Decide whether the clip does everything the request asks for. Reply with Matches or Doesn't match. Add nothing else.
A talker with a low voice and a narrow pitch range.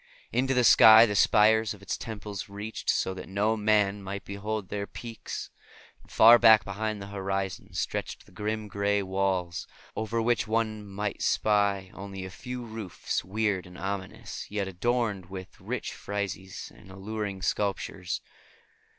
Matches